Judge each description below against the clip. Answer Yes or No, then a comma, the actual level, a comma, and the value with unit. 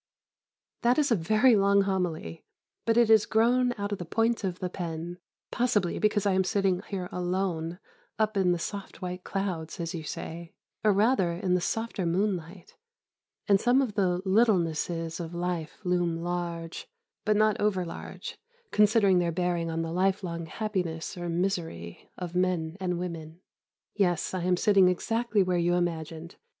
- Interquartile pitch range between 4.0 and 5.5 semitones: No, average, 3.2 semitones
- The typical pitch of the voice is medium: Yes, medium, 180 Hz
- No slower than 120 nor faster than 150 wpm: No, average, 165 wpm